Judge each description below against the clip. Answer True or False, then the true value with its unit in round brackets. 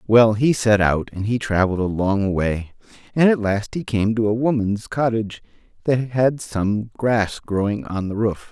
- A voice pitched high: False (110 Hz)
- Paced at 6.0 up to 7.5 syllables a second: False (4.4 syllables/s)